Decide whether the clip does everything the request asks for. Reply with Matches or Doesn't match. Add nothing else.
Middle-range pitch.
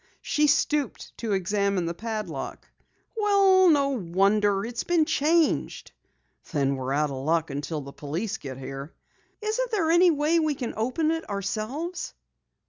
Doesn't match